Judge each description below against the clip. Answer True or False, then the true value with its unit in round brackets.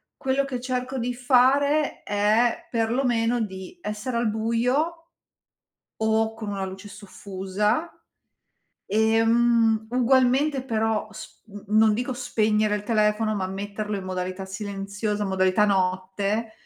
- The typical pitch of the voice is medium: False (220 Hz)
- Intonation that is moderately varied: True (3.2 semitones)